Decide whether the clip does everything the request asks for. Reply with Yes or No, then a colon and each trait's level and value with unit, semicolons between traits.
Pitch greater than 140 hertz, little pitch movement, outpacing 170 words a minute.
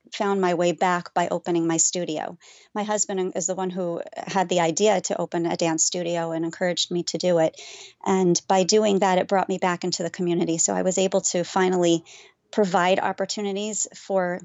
Yes: medium, 185 Hz; narrow, 2.0 semitones; average, 200 wpm